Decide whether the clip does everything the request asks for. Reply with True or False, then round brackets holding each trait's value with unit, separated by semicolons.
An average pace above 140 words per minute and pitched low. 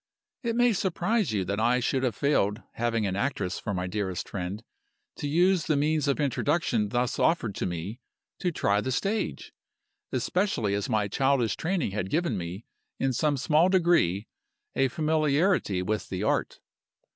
True (165 wpm; 125 Hz)